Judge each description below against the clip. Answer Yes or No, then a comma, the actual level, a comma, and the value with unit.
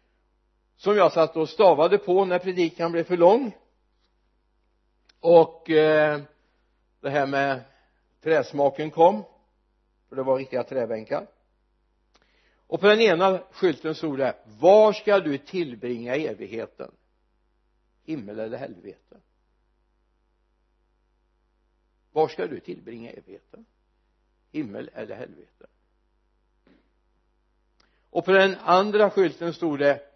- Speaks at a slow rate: Yes, slow, 105 wpm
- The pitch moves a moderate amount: No, wide, 7.6 semitones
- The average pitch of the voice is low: No, medium, 145 Hz